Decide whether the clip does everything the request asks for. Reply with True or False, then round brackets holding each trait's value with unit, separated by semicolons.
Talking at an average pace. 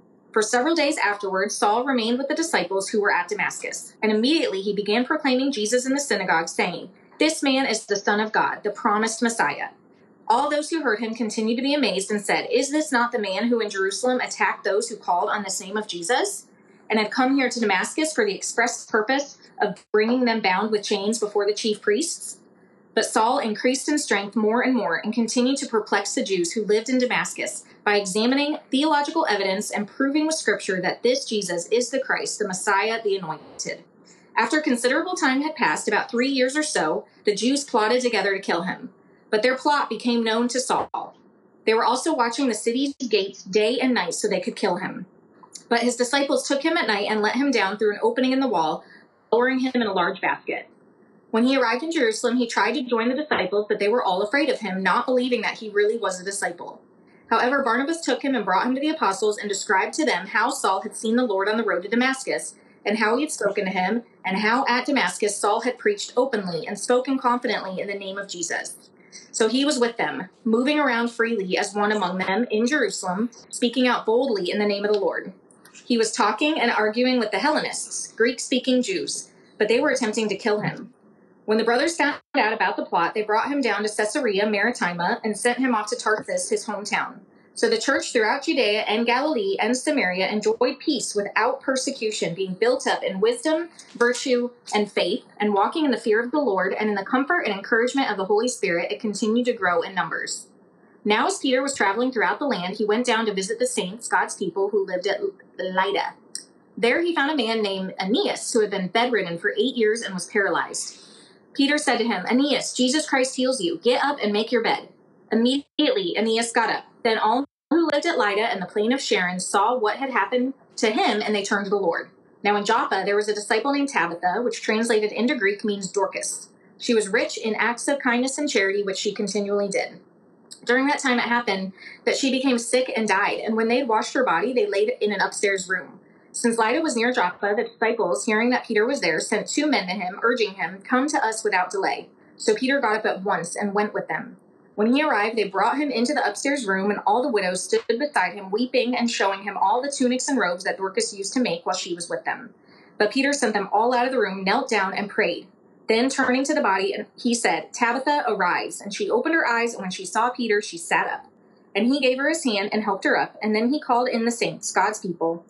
False (225 wpm)